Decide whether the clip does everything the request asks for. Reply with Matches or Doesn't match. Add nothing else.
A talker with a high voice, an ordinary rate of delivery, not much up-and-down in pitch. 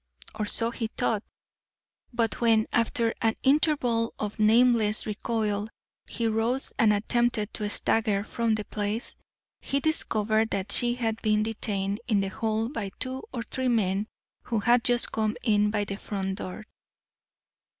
Matches